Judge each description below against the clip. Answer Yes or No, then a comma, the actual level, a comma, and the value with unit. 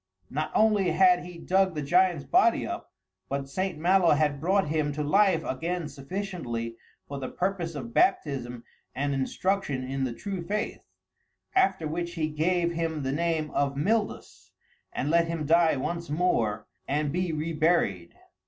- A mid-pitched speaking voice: Yes, medium, 160 Hz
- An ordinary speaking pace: Yes, average, 155 wpm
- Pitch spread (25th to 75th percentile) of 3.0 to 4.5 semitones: Yes, average, 4.2 semitones